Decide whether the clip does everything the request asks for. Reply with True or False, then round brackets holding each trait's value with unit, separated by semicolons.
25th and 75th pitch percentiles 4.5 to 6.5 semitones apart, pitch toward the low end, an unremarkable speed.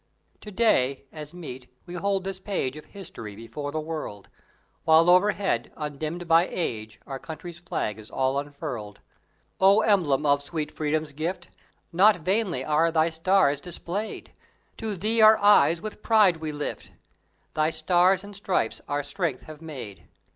False (4.8 semitones; 160 Hz; 155 wpm)